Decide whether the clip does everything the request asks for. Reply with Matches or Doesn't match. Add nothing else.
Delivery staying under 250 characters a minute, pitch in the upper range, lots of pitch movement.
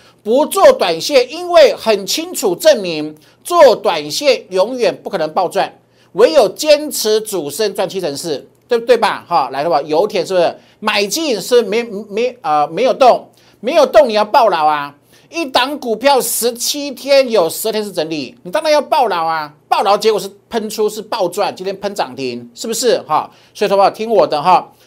Doesn't match